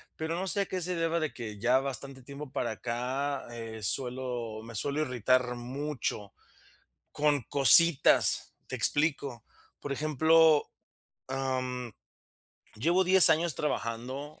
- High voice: No, low, 135 Hz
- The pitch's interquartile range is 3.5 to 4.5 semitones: Yes, average, 4.0 semitones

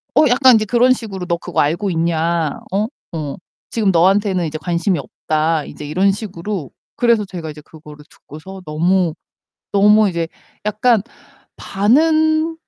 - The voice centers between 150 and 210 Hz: Yes, high, 190 Hz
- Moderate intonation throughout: Yes, average, 4.9 semitones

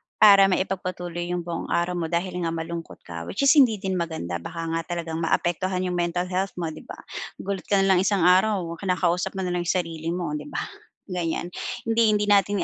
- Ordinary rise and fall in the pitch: No, narrow, 2.3 semitones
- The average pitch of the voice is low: No, medium, 180 Hz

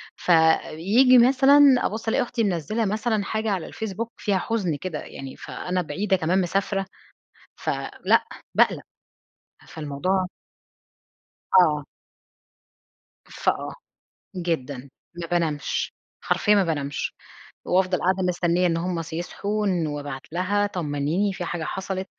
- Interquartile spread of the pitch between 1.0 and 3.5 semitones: No, average, 4.1 semitones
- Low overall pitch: No, medium, 185 Hz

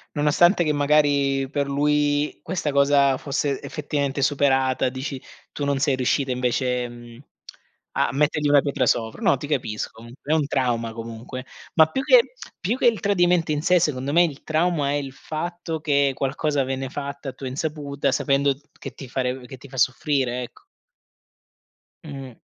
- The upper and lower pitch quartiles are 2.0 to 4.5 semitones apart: Yes, narrow, 2.4 semitones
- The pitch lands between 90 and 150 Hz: Yes, medium, 140 Hz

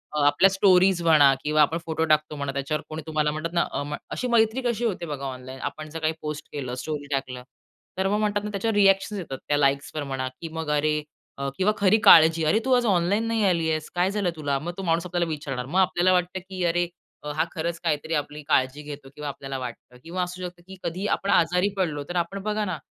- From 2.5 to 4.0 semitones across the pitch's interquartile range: No, average, 4.4 semitones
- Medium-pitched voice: Yes, medium, 165 Hz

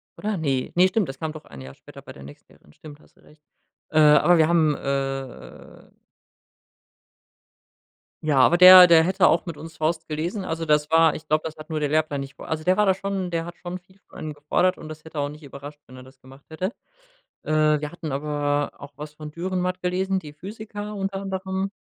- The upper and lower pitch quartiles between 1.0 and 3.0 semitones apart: No, average, 3.7 semitones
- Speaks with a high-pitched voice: No, medium, 155 Hz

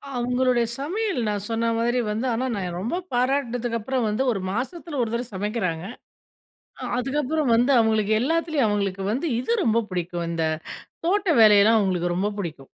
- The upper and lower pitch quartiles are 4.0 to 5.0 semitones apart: Yes, average, 4.3 semitones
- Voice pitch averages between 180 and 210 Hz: No, high, 230 Hz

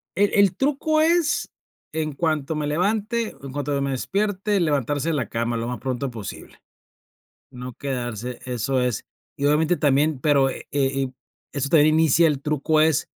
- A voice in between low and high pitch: Yes, medium, 145 Hz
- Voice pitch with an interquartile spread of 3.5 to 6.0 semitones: Yes, average, 4.0 semitones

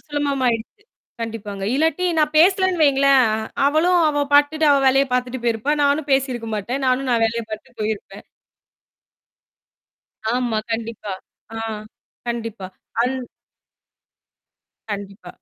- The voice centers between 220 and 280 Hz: Yes, very high, 255 Hz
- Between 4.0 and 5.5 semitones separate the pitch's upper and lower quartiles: Yes, average, 4.3 semitones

